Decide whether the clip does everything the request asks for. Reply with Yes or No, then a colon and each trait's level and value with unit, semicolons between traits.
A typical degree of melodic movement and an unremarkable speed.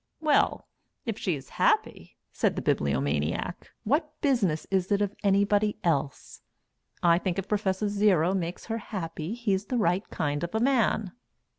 Yes: average, 4.1 semitones; average, 155 wpm